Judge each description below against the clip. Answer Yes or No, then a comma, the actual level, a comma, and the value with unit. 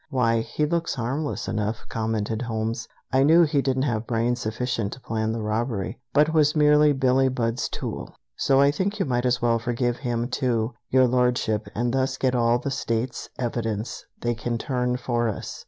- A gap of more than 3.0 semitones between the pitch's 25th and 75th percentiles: No, narrow, 2.6 semitones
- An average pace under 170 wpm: No, average, 185 wpm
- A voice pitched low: Yes, low, 120 Hz